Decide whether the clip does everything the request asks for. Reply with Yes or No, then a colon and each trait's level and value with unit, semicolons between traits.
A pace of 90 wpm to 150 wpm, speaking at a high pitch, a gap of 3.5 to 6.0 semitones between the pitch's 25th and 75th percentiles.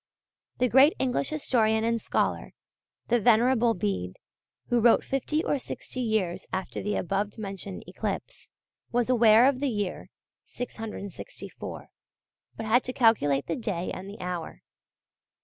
Yes: slow, 135 wpm; high, 225 Hz; average, 4.1 semitones